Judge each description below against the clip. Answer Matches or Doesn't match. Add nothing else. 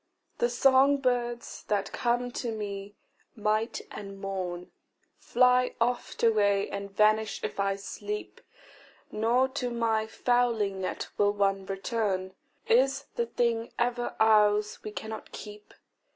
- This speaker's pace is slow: Matches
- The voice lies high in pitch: Matches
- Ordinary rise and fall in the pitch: Matches